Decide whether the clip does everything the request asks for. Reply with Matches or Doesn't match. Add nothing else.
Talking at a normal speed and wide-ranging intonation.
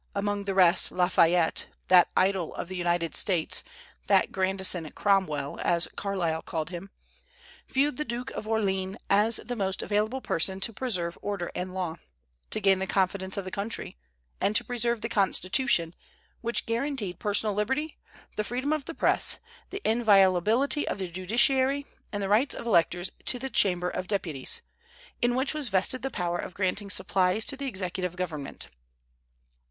Doesn't match